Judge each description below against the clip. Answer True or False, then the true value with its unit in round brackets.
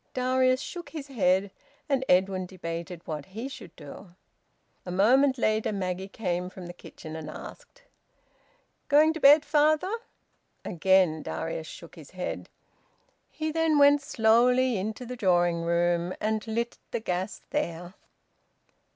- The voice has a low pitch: False (200 Hz)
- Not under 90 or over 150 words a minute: True (135 wpm)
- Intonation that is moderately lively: False (6.9 semitones)